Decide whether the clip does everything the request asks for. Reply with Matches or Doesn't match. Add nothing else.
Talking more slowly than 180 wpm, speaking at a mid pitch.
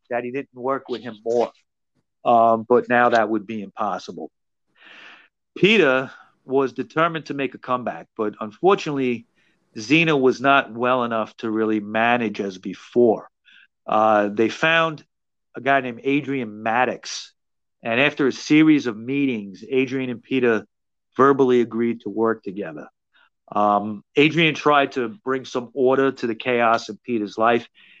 Doesn't match